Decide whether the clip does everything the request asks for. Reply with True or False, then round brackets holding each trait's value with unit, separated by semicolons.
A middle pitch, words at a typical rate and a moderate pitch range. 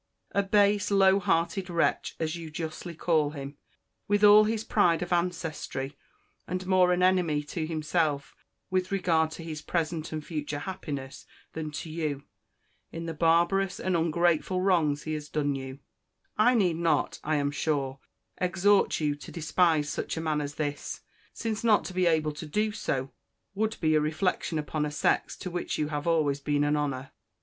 True (165 Hz; 175 wpm; 3.5 semitones)